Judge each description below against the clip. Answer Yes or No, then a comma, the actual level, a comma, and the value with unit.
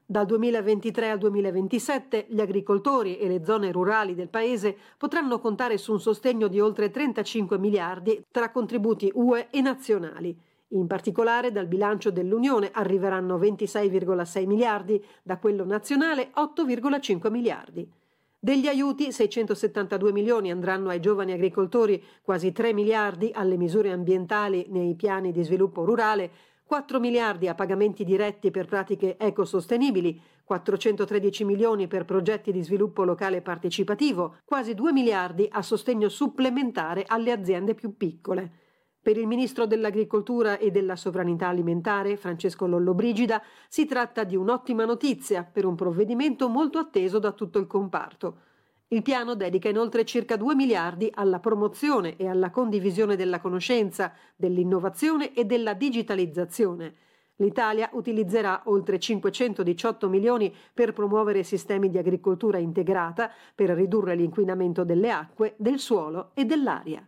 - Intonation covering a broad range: No, average, 3.4 semitones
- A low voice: No, high, 210 Hz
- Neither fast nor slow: Yes, average, 130 wpm